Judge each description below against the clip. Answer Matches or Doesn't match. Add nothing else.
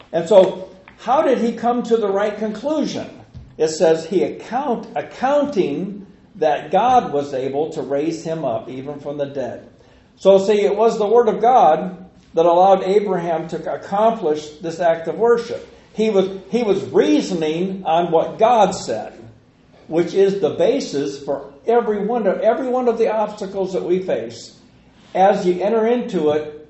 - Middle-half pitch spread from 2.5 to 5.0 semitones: Doesn't match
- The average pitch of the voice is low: Doesn't match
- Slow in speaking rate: Doesn't match